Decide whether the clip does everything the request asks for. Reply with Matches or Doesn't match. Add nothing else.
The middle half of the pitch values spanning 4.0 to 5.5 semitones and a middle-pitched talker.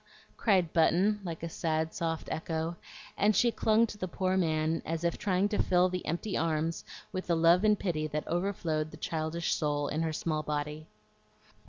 Doesn't match